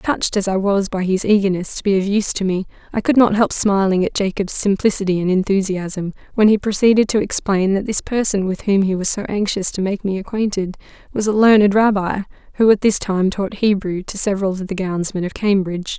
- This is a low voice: No, high, 195 Hz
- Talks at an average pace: No, fast, 220 wpm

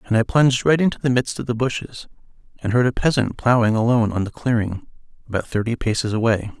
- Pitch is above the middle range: No, low, 115 Hz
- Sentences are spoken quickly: Yes, fast, 210 wpm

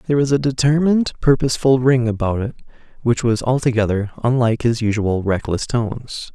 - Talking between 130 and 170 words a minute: Yes, average, 150 wpm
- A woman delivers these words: No, male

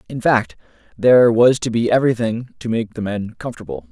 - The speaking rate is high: No, average, 185 wpm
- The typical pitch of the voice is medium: No, low, 115 Hz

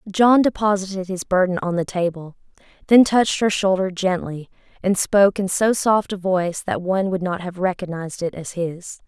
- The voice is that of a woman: Yes, female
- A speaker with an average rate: Yes, average, 185 wpm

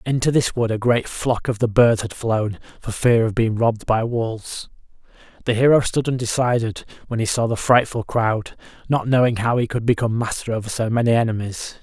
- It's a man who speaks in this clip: Yes, male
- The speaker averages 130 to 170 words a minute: No, average, 200 wpm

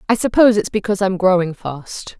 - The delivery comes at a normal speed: Yes, average, 190 wpm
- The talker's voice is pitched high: Yes, high, 195 Hz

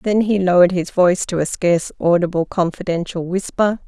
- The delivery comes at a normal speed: Yes, average, 170 wpm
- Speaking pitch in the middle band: Yes, medium, 180 Hz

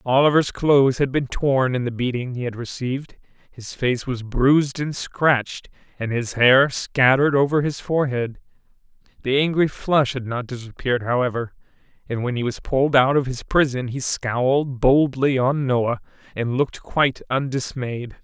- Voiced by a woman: No, male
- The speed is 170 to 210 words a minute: No, average, 160 wpm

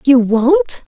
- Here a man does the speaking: No, female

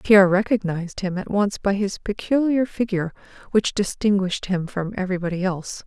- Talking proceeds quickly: No, average, 155 wpm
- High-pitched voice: Yes, high, 195 Hz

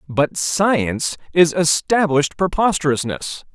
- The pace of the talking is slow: Yes, slow, 85 wpm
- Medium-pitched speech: Yes, medium, 160 Hz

